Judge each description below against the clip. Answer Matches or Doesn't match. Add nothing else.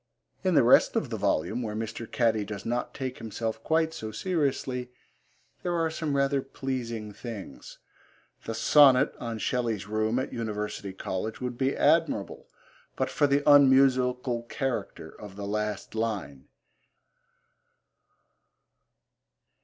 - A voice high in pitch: Doesn't match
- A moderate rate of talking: Doesn't match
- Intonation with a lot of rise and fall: Doesn't match